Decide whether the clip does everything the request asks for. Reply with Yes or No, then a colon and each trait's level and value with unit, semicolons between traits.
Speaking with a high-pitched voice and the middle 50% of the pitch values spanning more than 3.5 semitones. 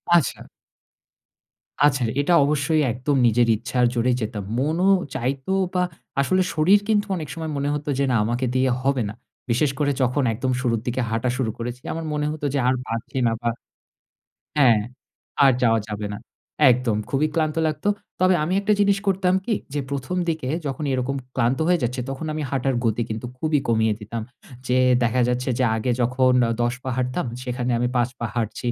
No: low, 130 Hz; average, 4.0 semitones